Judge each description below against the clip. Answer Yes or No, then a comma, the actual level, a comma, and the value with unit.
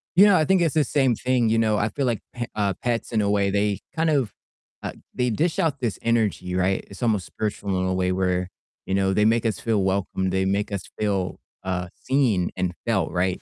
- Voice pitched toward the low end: Yes, low, 105 Hz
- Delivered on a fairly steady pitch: No, average, 4.2 semitones